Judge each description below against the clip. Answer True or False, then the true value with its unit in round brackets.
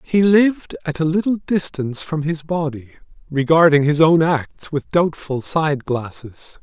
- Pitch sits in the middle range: True (155 Hz)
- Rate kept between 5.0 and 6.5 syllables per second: False (4.3 syllables/s)